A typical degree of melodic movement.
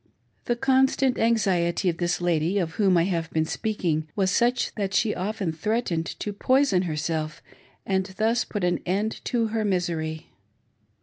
Yes: average, 4.7 semitones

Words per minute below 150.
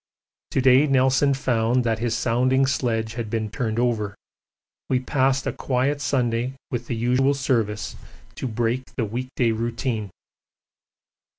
Yes: average, 140 wpm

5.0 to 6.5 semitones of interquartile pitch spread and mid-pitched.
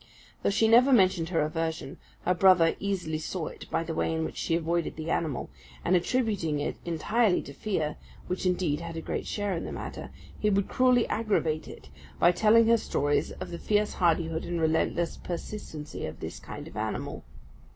No: average, 4.1 semitones; medium, 170 Hz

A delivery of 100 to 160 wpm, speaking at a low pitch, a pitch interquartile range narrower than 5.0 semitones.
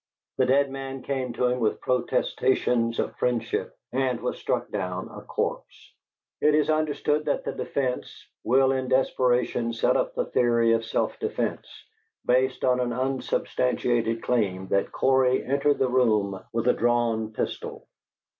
Yes: average, 150 wpm; low, 125 Hz; narrow, 2.4 semitones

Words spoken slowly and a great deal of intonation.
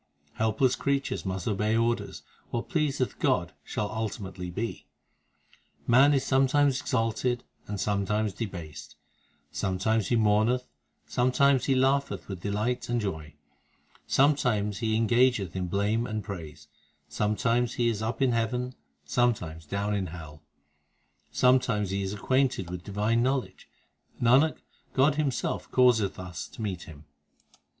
No: slow, 130 wpm; average, 4.2 semitones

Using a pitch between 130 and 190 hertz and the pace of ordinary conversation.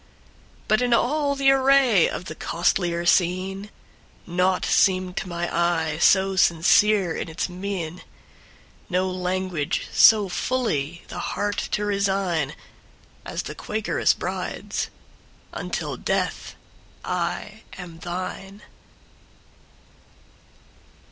No: medium, 185 Hz; slow, 90 wpm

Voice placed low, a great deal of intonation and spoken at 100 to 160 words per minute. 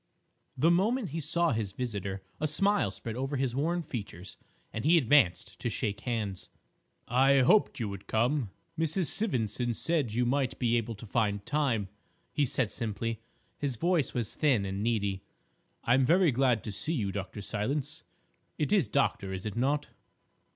No: low, 125 Hz; wide, 5.8 semitones; average, 170 wpm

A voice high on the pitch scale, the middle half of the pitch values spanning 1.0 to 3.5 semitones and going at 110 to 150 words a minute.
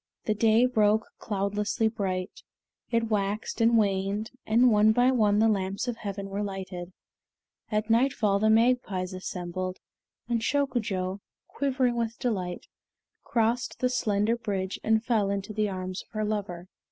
Yes: high, 215 Hz; average, 2.8 semitones; average, 145 wpm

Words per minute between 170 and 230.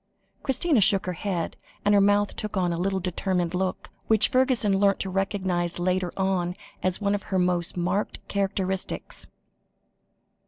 No: average, 155 wpm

